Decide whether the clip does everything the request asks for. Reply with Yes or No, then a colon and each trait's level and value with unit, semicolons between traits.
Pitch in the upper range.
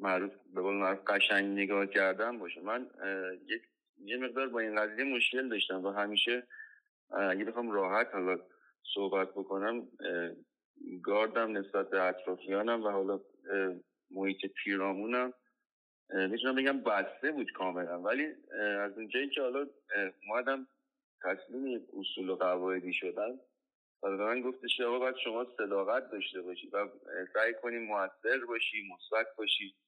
No: low, 100 Hz